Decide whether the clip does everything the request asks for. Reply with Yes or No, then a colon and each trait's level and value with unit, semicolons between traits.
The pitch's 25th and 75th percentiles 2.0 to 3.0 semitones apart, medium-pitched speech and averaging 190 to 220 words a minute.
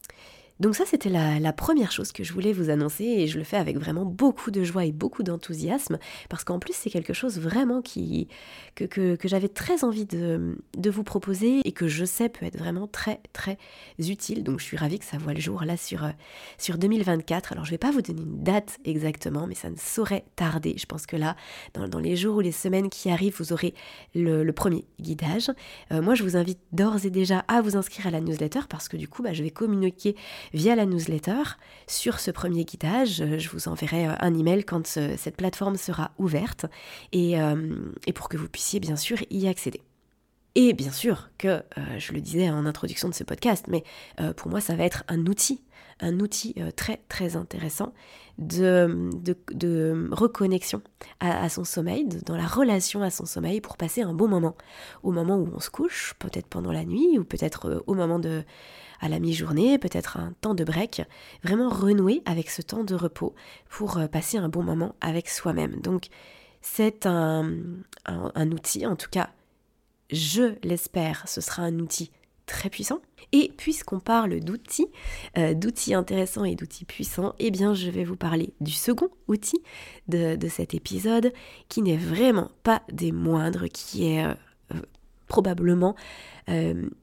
No: average, 4.3 semitones; medium, 180 Hz; average, 195 wpm